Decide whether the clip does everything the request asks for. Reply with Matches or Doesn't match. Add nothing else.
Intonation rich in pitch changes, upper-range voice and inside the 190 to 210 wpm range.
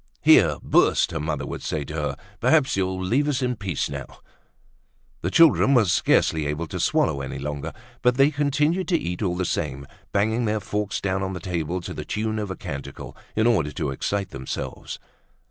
Doesn't match